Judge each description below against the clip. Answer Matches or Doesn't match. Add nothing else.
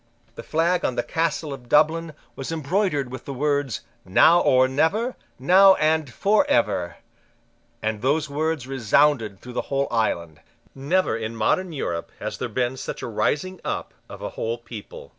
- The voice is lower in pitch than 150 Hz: Matches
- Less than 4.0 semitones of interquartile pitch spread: Doesn't match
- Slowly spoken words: Doesn't match